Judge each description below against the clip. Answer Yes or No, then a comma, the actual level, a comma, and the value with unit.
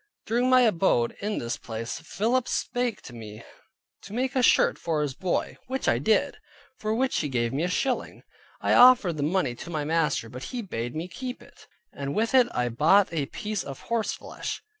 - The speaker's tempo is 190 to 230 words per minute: Yes, fast, 205 wpm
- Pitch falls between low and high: Yes, medium, 175 Hz